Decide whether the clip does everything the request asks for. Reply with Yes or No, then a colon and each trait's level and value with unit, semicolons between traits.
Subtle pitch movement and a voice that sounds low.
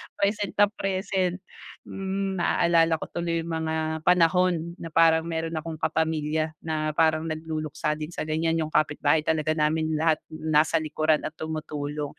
No: narrow, 1.3 semitones; medium, 160 Hz